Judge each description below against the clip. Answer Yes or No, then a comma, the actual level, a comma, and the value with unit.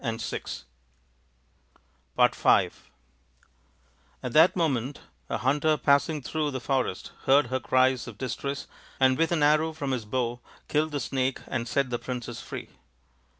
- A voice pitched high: No, low, 130 Hz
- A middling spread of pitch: Yes, average, 3.1 semitones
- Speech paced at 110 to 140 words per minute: No, average, 150 wpm